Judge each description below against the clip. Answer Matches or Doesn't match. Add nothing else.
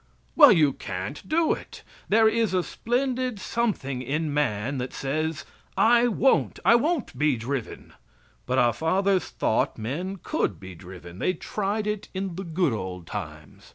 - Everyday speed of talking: Matches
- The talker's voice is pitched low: Doesn't match